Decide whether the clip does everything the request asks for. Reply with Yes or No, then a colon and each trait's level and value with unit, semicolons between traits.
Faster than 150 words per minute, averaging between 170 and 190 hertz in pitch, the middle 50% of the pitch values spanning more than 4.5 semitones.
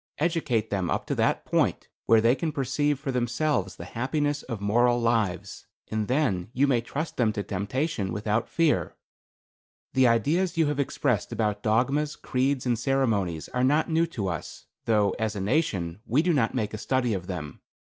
No: average, 180 wpm; low, 120 Hz; wide, 5.5 semitones